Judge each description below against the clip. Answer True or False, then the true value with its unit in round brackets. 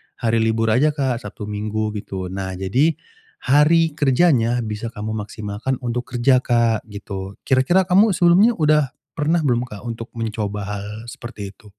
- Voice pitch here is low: True (120 Hz)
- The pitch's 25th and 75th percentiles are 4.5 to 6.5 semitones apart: True (5.5 semitones)